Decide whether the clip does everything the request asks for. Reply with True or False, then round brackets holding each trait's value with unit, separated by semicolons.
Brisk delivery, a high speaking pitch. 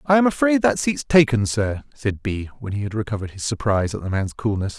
False (240 wpm; 115 Hz)